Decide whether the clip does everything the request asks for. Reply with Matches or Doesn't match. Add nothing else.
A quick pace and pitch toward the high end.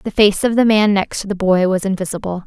Matches